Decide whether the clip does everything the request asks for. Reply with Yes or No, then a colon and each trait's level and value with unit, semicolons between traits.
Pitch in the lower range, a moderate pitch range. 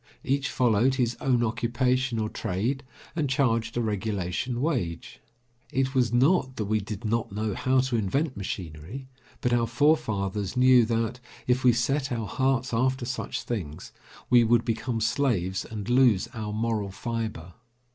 Yes: low, 120 Hz; average, 3.2 semitones